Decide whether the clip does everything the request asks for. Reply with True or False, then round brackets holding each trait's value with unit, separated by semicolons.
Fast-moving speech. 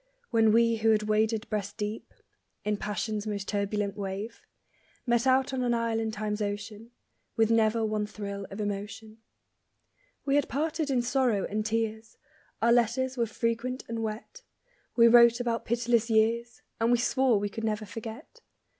False (165 wpm)